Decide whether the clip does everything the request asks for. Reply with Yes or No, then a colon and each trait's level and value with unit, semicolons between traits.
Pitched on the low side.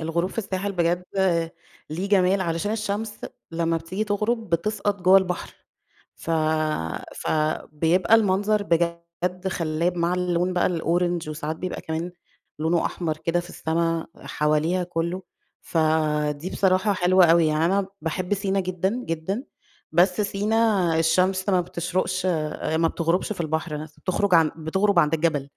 No: medium, 175 Hz